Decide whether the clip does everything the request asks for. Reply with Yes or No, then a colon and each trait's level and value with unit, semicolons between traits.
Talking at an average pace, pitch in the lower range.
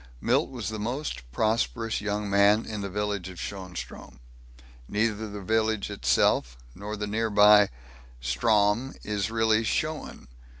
No: slow, 130 wpm; low, 105 Hz